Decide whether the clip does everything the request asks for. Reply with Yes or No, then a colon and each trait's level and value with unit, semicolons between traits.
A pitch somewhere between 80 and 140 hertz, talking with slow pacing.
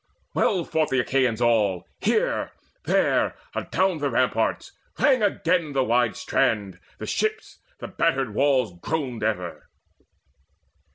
Yes: low, 135 Hz; slow, 125 wpm